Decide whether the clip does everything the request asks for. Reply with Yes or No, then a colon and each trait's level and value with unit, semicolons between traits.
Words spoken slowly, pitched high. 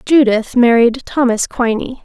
Yes: slow, 120 wpm; high, 240 Hz